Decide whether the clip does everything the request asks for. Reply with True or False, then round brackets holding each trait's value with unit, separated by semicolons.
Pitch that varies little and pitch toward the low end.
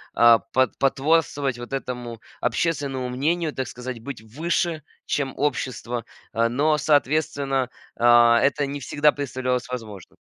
False (3.1 semitones; 130 Hz)